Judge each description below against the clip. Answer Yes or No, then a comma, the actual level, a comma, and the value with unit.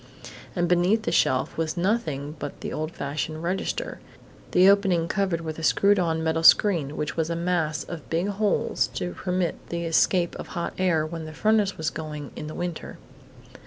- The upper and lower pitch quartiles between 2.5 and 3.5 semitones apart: Yes, average, 2.8 semitones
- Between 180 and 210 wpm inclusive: Yes, average, 185 wpm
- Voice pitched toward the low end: No, medium, 170 Hz